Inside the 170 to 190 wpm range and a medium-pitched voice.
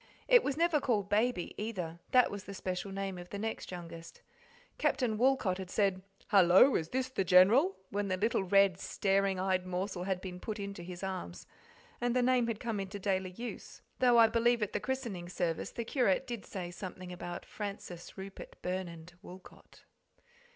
No: average, 180 wpm; high, 195 Hz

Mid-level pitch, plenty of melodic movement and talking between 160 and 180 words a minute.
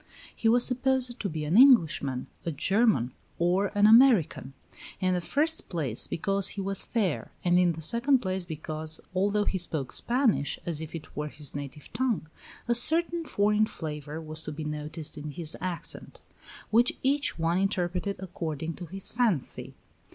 Yes: medium, 180 Hz; wide, 6.1 semitones; average, 165 wpm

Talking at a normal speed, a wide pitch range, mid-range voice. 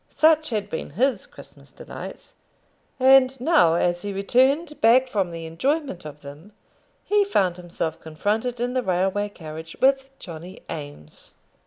No: average, 145 wpm; wide, 7.9 semitones; high, 205 Hz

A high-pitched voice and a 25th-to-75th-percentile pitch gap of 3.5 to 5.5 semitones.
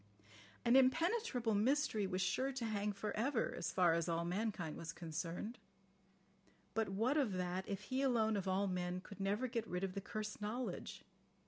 Yes: high, 210 Hz; average, 4.6 semitones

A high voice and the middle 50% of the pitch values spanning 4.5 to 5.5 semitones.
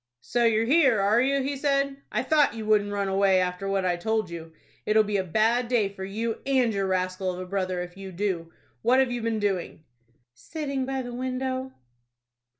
Yes: high, 215 Hz; average, 5.1 semitones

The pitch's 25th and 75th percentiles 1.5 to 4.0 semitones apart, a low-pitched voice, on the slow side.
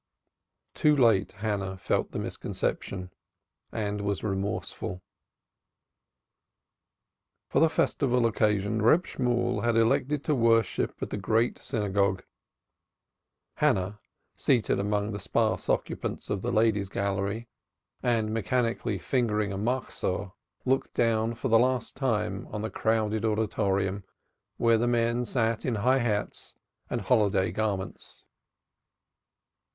Yes: average, 2.8 semitones; low, 110 Hz; slow, 115 wpm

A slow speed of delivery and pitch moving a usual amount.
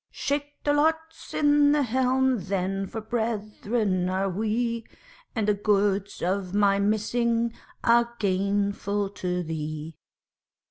Yes: slow, 120 wpm; average, 3.4 semitones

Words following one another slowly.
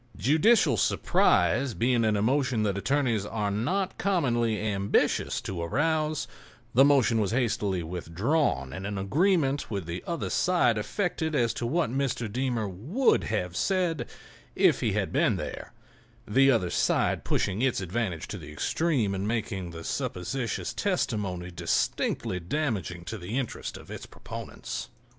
No: average, 145 wpm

